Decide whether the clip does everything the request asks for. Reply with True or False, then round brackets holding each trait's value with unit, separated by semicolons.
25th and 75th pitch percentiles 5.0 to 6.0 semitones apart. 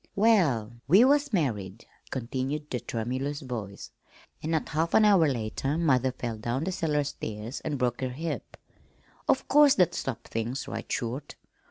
True (5.5 semitones)